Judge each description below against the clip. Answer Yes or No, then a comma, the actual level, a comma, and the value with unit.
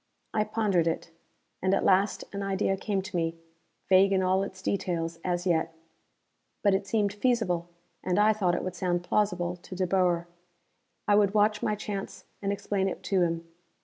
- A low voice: No, high, 190 Hz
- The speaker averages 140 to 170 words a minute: No, average, 180 wpm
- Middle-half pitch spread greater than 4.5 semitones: No, narrow, 2.5 semitones